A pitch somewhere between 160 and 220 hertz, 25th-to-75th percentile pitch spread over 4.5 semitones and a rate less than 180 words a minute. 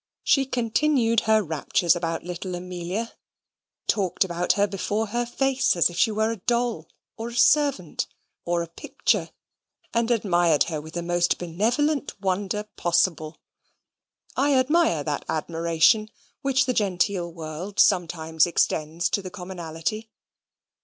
Yes: medium, 185 Hz; average, 5.2 semitones; slow, 135 wpm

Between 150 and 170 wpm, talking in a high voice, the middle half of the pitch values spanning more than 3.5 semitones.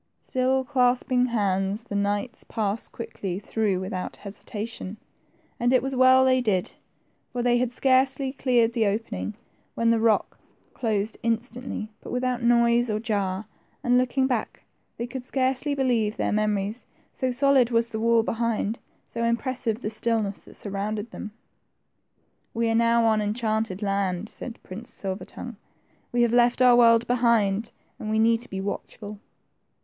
No: average, 155 wpm; high, 230 Hz; average, 2.7 semitones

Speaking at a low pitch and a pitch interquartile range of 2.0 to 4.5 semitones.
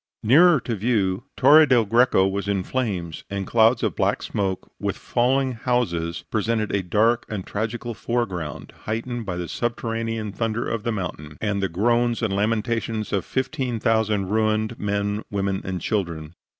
Yes: low, 110 Hz; average, 3.3 semitones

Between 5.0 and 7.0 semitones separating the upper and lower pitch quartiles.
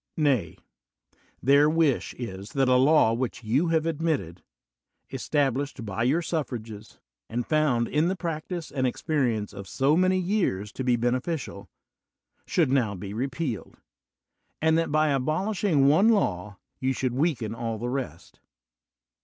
Yes: wide, 5.5 semitones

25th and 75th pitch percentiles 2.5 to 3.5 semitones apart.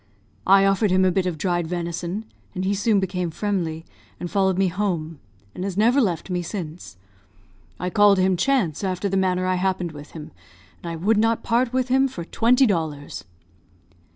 Yes: average, 3.0 semitones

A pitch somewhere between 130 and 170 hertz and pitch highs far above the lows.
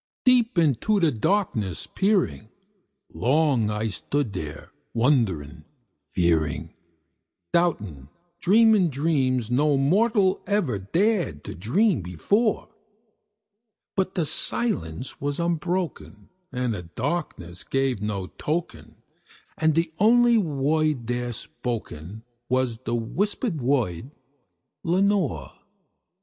Yes: medium, 140 Hz; wide, 9.0 semitones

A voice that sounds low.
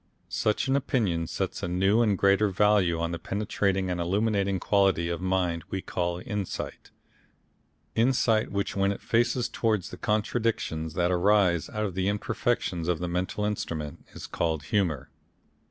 Yes: very low, 95 Hz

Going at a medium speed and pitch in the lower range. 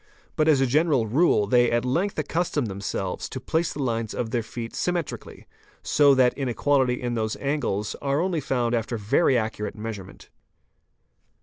Yes: average, 170 wpm; low, 125 Hz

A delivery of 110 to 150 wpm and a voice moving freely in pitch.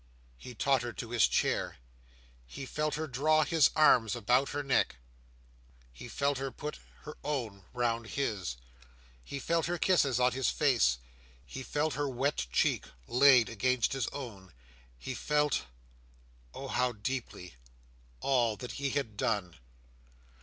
Yes: slow, 135 wpm; wide, 5.9 semitones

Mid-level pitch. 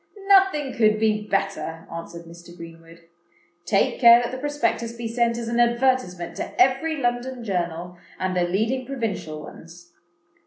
No: high, 220 Hz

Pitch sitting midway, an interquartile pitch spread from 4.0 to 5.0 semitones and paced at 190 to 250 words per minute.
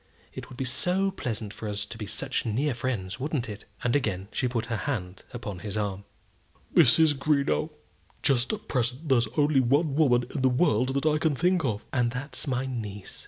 No: low, 125 Hz; average, 4.6 semitones; average, 200 wpm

